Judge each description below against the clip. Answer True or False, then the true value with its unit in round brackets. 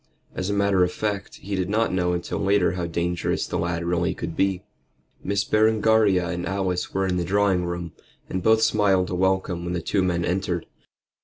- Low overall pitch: True (95 Hz)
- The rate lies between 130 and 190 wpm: False (200 wpm)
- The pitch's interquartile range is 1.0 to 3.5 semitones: True (2.4 semitones)